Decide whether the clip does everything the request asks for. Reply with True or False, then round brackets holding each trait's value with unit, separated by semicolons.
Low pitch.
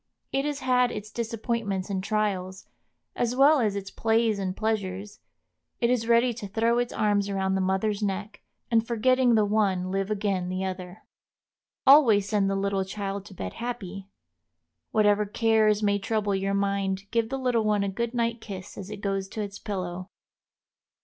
False (205 Hz)